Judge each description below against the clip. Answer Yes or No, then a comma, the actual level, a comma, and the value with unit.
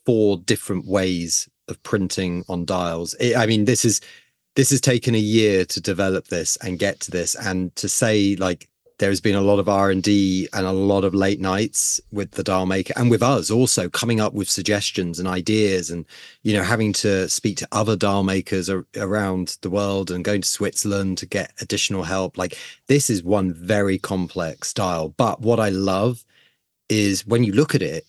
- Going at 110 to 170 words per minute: No, fast, 205 wpm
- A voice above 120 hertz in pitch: No, low, 100 Hz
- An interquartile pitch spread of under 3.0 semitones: Yes, narrow, 2.6 semitones